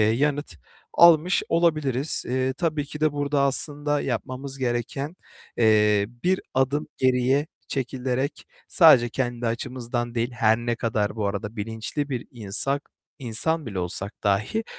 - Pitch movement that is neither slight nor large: Yes, average, 4.3 semitones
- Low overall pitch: Yes, low, 130 Hz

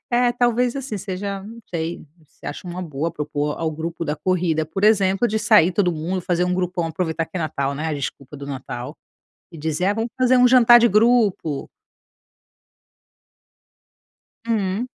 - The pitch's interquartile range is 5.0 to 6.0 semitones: Yes, average, 5.3 semitones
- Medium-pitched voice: Yes, medium, 180 Hz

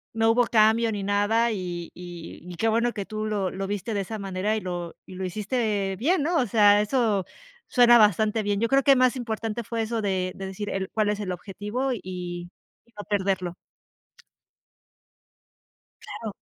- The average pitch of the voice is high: Yes, high, 210 Hz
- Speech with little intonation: No, average, 3.1 semitones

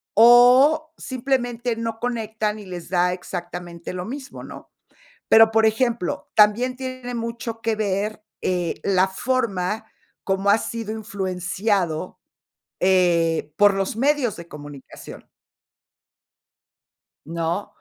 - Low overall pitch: No, high, 215 Hz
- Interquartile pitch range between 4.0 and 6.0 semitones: Yes, average, 4.6 semitones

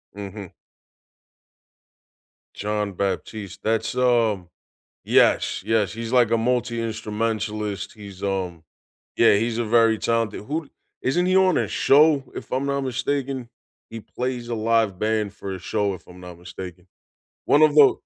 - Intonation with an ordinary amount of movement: Yes, average, 3.6 semitones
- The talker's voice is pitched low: Yes, low, 110 Hz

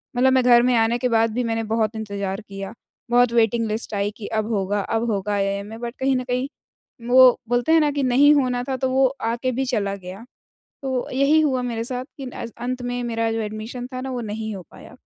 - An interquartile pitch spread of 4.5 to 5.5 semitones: No, average, 2.7 semitones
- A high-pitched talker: Yes, high, 235 Hz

